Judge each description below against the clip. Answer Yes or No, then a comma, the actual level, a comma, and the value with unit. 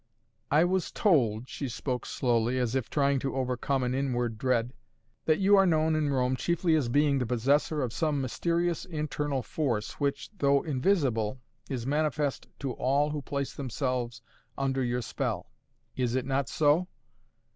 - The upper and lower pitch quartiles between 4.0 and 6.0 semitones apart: No, average, 3.2 semitones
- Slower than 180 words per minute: Yes, average, 160 wpm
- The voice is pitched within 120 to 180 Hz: Yes, low, 135 Hz